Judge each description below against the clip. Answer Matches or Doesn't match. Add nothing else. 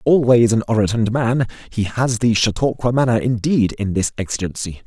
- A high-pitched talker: Doesn't match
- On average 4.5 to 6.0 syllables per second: Matches